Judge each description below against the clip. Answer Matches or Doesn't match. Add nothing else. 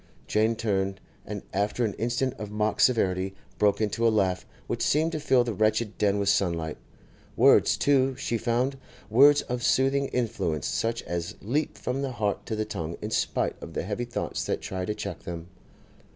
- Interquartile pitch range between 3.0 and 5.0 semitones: Matches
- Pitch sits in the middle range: Doesn't match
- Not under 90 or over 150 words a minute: Doesn't match